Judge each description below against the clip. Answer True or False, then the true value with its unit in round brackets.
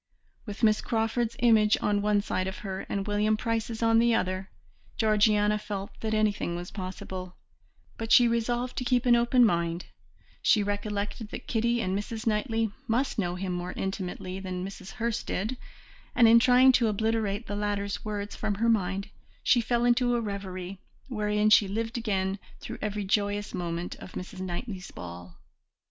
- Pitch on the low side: False (210 Hz)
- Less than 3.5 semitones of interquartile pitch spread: True (2.9 semitones)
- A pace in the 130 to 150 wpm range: False (170 wpm)